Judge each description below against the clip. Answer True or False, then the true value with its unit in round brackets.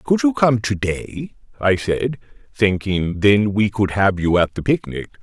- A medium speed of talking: True (185 wpm)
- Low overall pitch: True (105 Hz)